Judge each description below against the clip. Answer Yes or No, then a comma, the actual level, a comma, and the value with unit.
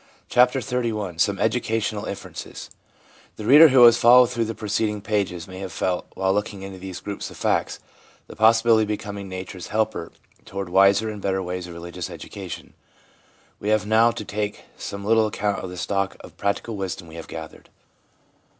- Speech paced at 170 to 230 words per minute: Yes, average, 175 wpm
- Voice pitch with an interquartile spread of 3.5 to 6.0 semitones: No, narrow, 2.6 semitones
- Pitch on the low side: Yes, low, 100 Hz